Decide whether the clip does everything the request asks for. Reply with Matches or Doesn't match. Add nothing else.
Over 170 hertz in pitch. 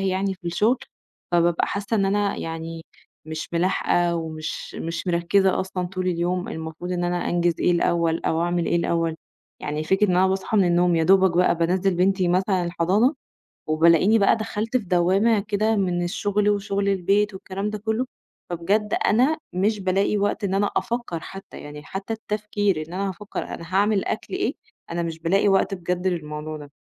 Matches